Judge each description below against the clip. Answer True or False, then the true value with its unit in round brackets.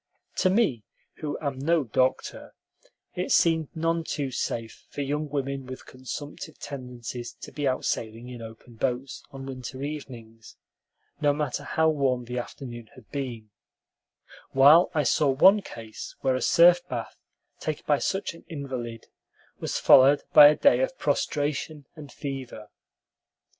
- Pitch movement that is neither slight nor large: True (3.4 semitones)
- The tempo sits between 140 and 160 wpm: True (145 wpm)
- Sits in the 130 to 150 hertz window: True (135 Hz)